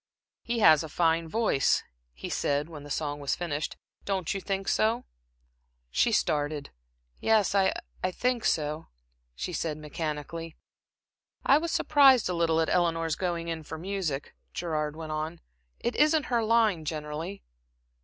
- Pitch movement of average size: Yes, average, 4.7 semitones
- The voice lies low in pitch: No, medium, 165 Hz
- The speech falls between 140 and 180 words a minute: Yes, average, 150 wpm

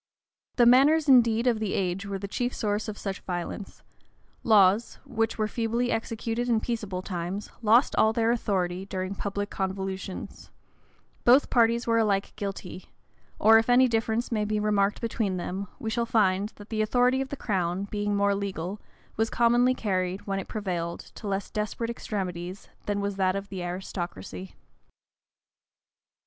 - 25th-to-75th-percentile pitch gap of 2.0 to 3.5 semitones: Yes, average, 3.1 semitones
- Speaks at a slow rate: No, average, 160 wpm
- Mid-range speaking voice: No, high, 205 Hz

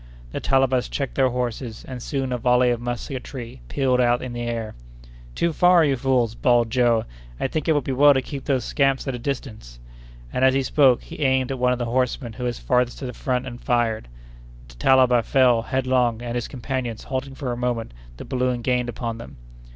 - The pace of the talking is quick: Yes, fast, 215 wpm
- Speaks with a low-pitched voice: Yes, low, 125 Hz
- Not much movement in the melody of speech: Yes, narrow, 1.8 semitones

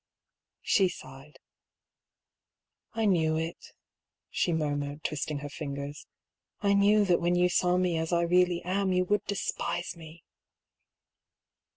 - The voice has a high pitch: No, medium, 170 Hz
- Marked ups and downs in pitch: No, average, 3.1 semitones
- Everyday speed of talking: No, slow, 130 wpm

